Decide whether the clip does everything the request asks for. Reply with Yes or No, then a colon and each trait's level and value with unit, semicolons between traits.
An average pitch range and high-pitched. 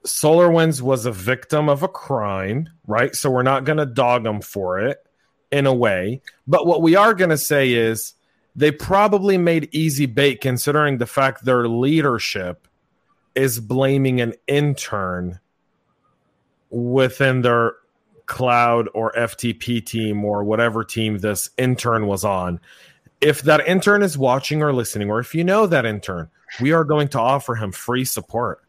No: average, 4.7 semitones; low, 130 Hz